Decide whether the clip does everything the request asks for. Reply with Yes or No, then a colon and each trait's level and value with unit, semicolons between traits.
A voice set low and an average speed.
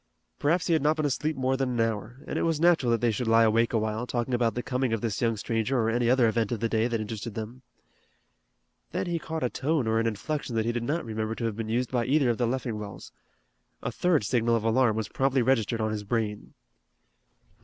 No: low, 120 Hz; fast, 245 wpm